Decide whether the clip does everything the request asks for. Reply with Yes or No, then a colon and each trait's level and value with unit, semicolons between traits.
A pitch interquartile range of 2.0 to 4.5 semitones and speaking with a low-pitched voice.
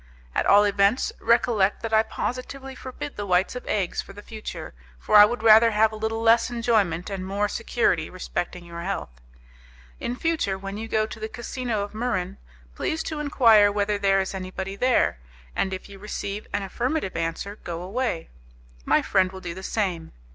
No: average, 3.2 semitones; high, 205 Hz